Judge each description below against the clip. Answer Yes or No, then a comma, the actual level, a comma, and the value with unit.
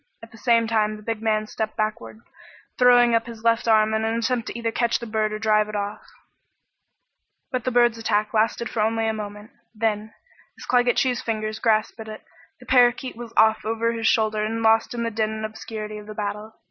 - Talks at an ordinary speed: No, fast, 215 wpm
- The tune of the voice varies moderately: No, narrow, 1.4 semitones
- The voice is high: Yes, high, 220 Hz